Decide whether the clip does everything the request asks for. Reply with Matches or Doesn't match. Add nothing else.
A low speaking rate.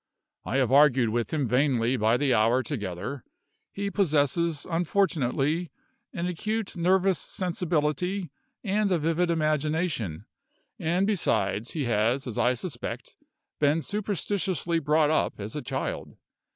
Matches